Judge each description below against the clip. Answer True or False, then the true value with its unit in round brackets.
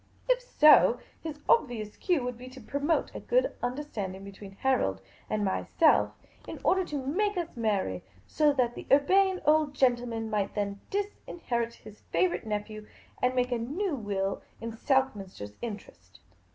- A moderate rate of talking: True (160 wpm)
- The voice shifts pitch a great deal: True (6.4 semitones)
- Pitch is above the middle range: True (245 Hz)